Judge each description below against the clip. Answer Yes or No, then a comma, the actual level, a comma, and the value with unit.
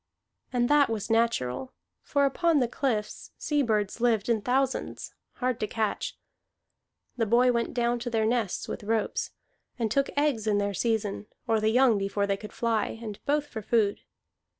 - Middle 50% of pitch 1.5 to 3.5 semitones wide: Yes, average, 2.9 semitones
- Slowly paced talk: No, average, 175 wpm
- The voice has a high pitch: Yes, high, 230 Hz